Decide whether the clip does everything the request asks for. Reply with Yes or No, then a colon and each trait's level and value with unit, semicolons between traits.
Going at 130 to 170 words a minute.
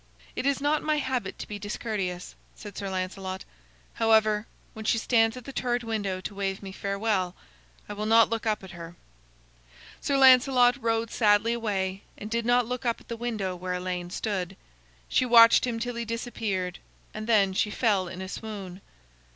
No: average, 185 wpm